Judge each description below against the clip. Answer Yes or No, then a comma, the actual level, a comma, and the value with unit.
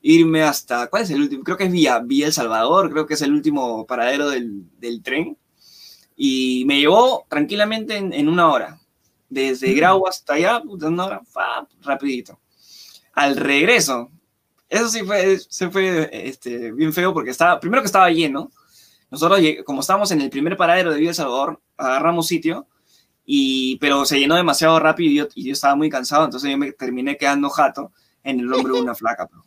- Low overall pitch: No, medium, 150 Hz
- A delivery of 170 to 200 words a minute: Yes, fast, 190 wpm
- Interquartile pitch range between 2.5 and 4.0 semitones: No, wide, 5.4 semitones